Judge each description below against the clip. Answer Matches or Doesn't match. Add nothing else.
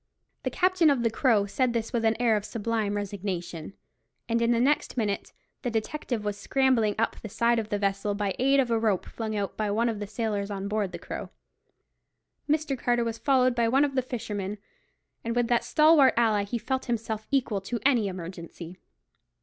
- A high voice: Matches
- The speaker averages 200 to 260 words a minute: Matches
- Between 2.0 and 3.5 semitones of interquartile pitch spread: Matches